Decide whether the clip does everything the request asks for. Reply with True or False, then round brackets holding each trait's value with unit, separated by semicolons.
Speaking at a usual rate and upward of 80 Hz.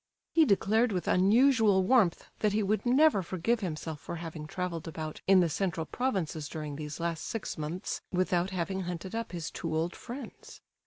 True (175 wpm; 185 Hz)